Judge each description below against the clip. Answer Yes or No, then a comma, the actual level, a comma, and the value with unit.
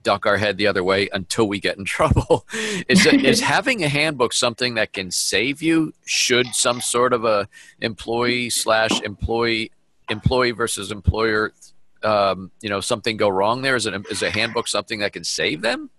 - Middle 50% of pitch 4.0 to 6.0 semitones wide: No, average, 3.3 semitones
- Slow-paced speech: No, average, 185 wpm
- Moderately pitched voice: No, low, 115 Hz